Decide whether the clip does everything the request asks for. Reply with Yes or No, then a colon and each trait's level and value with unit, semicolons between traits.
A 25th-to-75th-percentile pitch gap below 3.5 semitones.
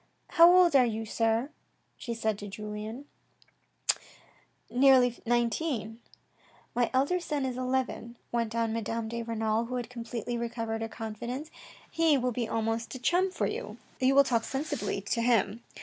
Yes: narrow, 2.6 semitones